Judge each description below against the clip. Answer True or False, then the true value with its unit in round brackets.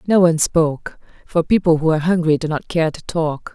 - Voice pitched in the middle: True (165 Hz)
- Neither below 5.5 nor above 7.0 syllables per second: True (5.7 syllables/s)